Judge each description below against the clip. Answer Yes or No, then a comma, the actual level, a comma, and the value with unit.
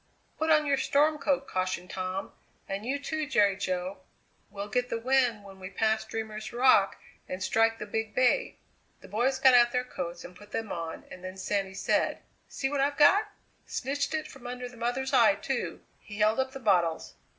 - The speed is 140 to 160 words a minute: No, average, 195 wpm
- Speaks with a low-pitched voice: No, high, 225 Hz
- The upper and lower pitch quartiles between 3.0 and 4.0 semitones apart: No, wide, 5.4 semitones